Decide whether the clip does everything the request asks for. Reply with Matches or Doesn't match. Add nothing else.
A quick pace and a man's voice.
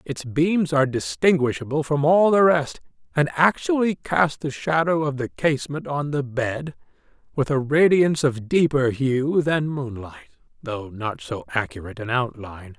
Doesn't match